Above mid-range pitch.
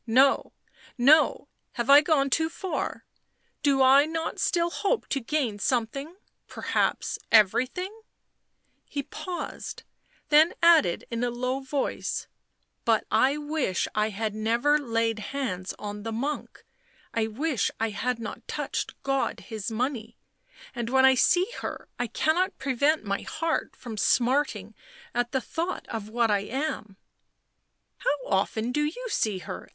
Yes: very high, 260 Hz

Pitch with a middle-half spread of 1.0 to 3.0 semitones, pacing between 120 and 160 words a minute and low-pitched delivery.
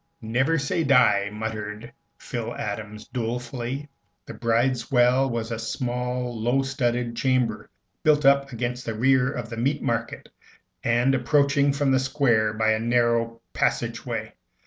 Yes: narrow, 2.6 semitones; average, 145 wpm; low, 120 Hz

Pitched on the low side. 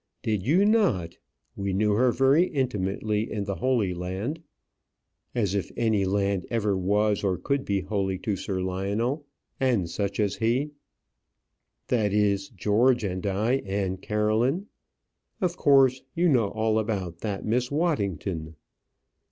Yes: low, 105 Hz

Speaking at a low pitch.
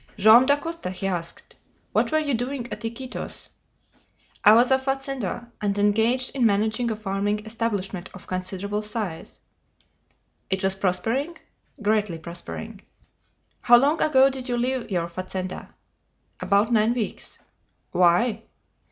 No: high, 220 Hz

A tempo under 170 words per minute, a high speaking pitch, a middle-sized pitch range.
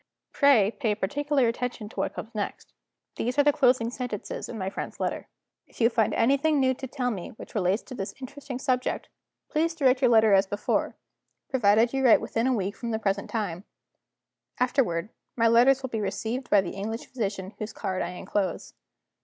No: average, 185 wpm; high, 230 Hz; average, 4.3 semitones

